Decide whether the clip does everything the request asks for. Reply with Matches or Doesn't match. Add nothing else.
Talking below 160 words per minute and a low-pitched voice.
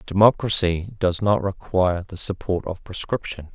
Matches